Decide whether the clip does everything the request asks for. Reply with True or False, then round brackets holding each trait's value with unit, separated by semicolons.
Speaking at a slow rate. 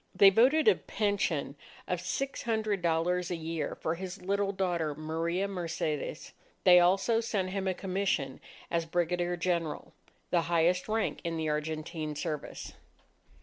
False (145 wpm)